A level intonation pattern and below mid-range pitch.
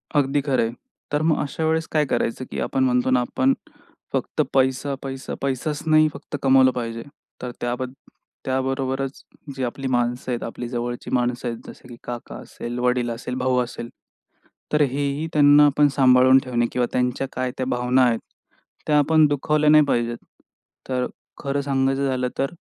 Yes: narrow, 2.3 semitones; low, 130 Hz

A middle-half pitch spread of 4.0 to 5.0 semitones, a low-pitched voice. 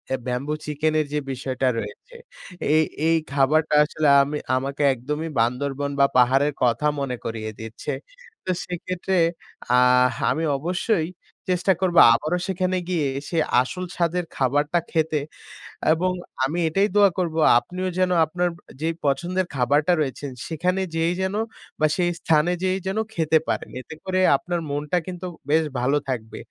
No: average, 4.6 semitones; medium, 155 Hz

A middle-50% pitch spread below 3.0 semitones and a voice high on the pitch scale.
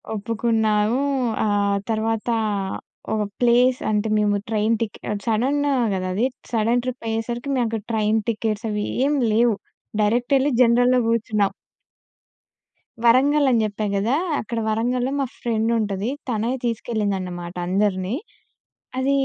Yes: narrow, 2.4 semitones; high, 225 Hz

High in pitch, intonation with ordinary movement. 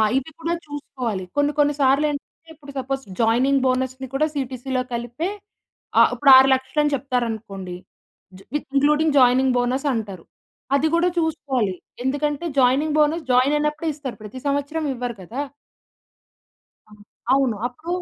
Yes: very high, 270 Hz; average, 3.0 semitones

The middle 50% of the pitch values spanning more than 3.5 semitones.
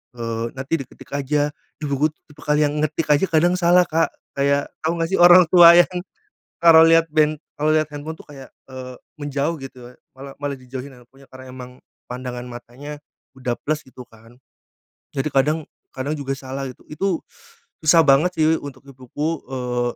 No: average, 3.2 semitones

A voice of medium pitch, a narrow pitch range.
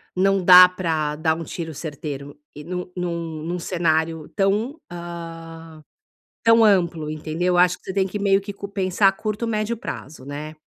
No: medium, 175 Hz; average, 3.4 semitones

